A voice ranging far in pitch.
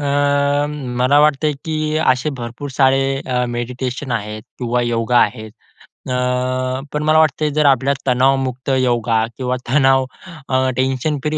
No: average, 2.7 semitones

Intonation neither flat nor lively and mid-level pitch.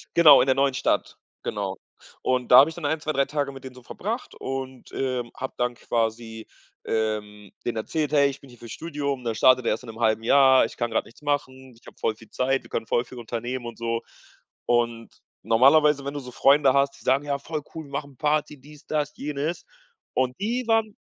No: average, 3.5 semitones; low, 130 Hz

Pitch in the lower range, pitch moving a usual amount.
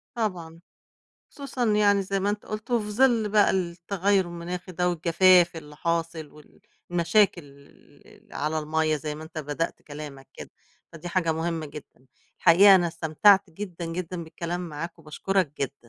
No: medium, 170 Hz; average, 3.5 semitones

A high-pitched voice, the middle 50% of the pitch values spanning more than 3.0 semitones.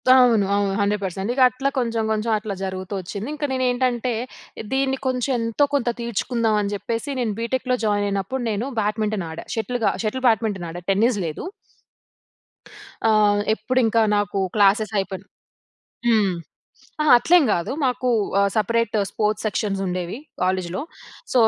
Yes: high, 220 Hz; average, 3.6 semitones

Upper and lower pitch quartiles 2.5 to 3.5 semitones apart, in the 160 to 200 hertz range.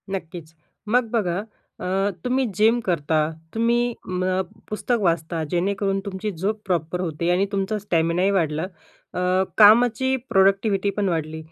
No: average, 3.9 semitones; high, 190 Hz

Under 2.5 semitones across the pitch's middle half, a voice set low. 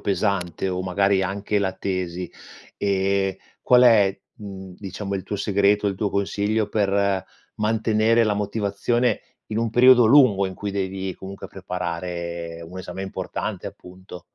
Yes: narrow, 1.8 semitones; low, 100 Hz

